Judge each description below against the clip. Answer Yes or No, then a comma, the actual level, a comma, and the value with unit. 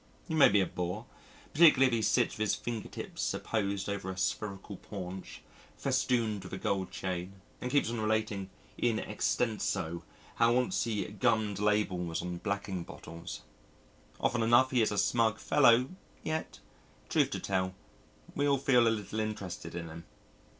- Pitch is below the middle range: Yes, low, 105 Hz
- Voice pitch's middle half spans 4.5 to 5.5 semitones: No, average, 3.7 semitones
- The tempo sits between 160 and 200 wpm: Yes, average, 165 wpm